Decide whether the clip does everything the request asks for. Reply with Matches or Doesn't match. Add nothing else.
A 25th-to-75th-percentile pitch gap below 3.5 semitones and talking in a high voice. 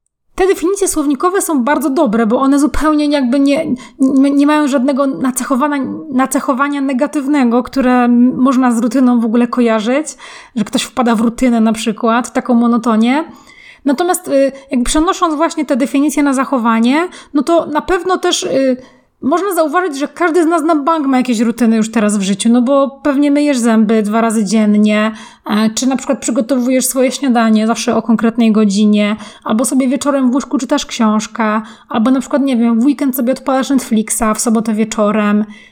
Doesn't match